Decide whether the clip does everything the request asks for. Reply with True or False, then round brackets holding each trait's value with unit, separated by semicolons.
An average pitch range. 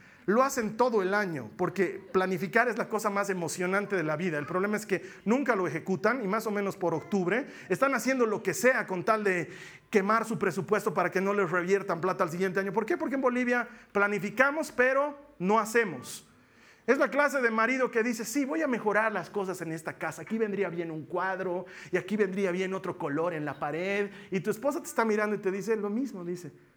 True (3.8 semitones)